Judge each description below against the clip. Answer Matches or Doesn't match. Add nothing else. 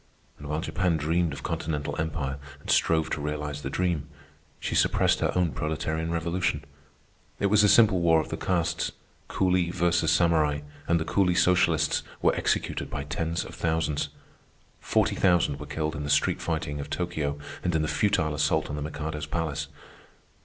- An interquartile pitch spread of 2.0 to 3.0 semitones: Matches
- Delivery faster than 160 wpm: Matches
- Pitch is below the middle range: Matches